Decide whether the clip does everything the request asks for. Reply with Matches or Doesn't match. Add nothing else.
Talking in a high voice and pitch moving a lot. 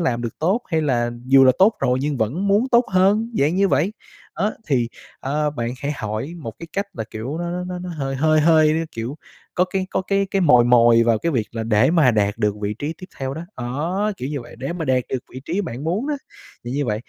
Doesn't match